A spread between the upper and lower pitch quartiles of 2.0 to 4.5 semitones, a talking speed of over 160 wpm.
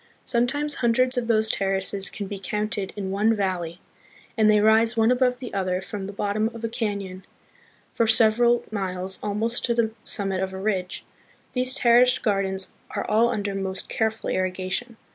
Yes: average, 3.2 semitones; average, 170 wpm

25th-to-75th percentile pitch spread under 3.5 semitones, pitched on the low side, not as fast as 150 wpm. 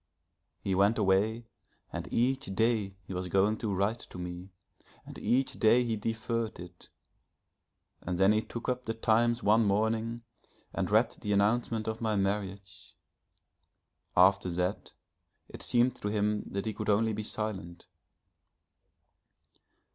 Yes: average, 2.7 semitones; low, 105 Hz; average, 140 wpm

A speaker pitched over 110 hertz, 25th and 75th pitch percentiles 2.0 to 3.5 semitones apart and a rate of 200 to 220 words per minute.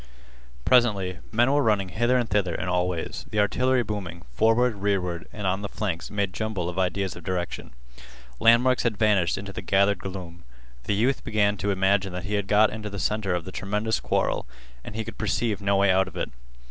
No: low, 100 Hz; average, 2.8 semitones; fast, 205 wpm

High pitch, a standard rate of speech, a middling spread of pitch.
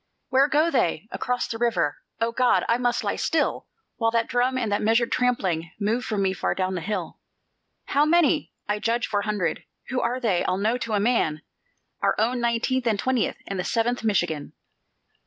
Yes: high, 230 Hz; average, 195 wpm; average, 3.6 semitones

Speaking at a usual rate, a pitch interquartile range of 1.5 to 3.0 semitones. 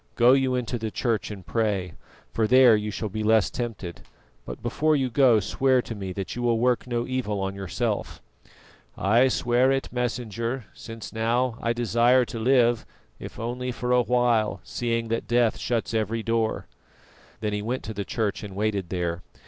Yes: average, 180 wpm; narrow, 2.5 semitones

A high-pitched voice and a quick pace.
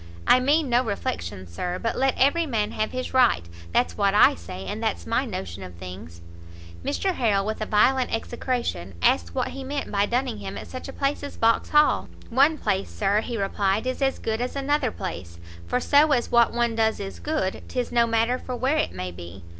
Yes: high, 230 Hz; fast, 210 wpm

